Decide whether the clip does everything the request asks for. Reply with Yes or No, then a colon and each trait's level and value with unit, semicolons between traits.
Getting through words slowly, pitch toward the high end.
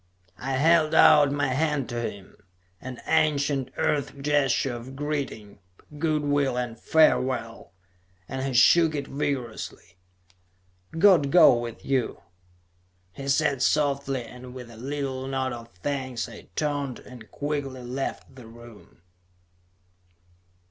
No: slow, 125 wpm; low, 135 Hz